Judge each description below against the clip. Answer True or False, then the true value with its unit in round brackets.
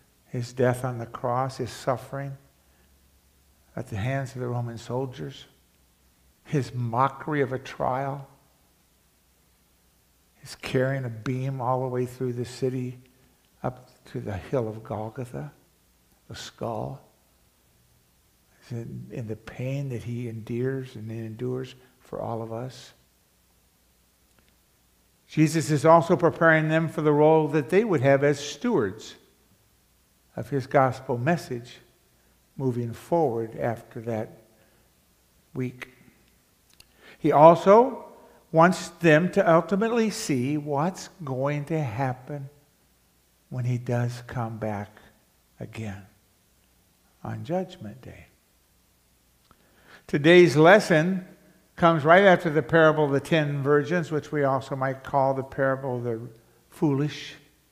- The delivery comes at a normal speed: False (115 wpm)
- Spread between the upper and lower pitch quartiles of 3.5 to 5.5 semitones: True (5.1 semitones)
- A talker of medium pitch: False (130 Hz)